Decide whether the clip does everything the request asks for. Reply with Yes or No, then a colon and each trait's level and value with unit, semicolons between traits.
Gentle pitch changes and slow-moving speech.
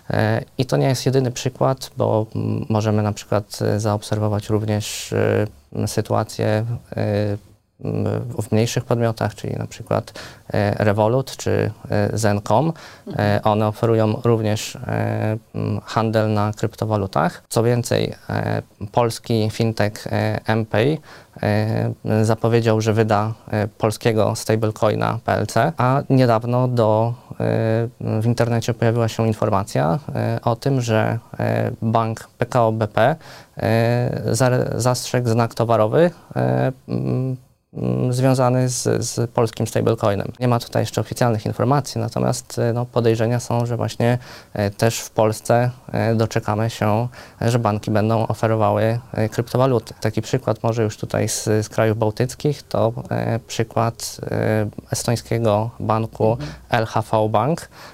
Yes: narrow, 1.9 semitones; slow, 105 wpm